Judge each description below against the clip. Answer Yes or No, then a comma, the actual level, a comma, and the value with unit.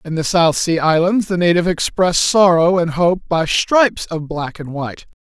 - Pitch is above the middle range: No, medium, 170 Hz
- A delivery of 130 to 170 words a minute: No, average, 195 wpm